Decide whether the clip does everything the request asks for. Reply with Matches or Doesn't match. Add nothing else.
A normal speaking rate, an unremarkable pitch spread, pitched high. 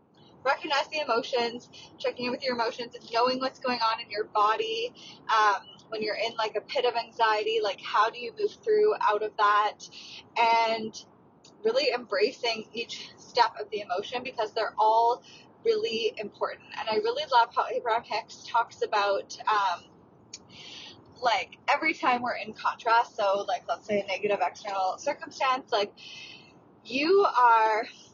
Matches